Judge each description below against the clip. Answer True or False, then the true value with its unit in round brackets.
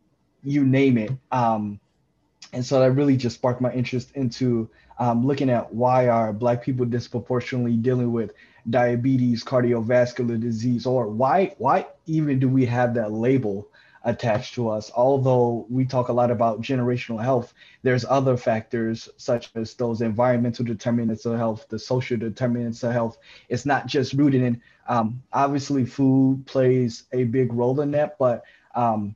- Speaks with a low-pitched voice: True (125 Hz)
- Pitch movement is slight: True (2.0 semitones)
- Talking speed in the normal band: True (160 wpm)